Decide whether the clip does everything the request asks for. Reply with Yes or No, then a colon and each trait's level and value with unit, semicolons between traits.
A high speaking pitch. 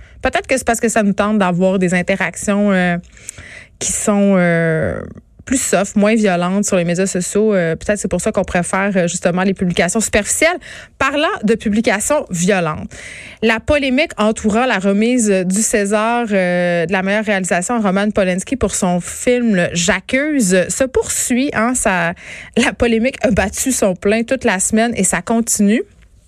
Yes: high, 210 Hz